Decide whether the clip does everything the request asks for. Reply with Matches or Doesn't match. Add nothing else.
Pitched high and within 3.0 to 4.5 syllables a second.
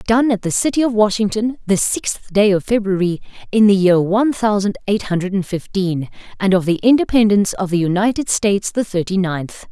Doesn't match